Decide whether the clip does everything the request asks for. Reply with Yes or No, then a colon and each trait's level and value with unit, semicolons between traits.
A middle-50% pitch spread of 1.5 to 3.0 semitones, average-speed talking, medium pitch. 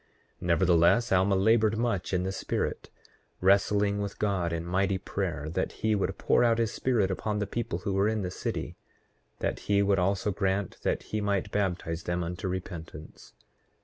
No: narrow, 2.4 semitones; average, 180 wpm; very low, 95 Hz